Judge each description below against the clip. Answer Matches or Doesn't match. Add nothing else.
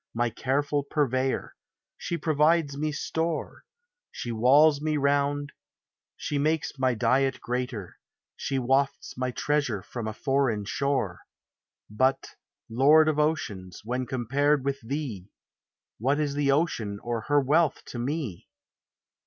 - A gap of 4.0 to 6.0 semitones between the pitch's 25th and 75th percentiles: Doesn't match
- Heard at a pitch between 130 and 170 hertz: Matches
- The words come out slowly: Matches